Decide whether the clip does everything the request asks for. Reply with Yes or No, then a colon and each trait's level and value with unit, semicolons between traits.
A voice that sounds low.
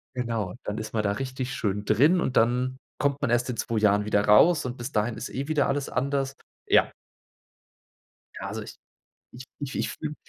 Yes: low, 125 Hz